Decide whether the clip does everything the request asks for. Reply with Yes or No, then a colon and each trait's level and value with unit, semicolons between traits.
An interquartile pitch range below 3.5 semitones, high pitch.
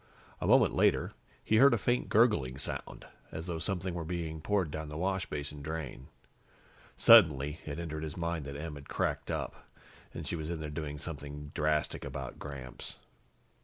No: average, 2.9 semitones; very low, 80 Hz